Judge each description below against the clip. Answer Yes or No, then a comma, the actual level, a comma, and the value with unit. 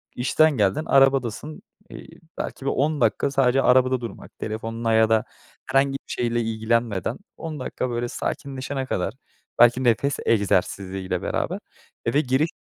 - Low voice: Yes, low, 125 Hz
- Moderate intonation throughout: Yes, average, 3.4 semitones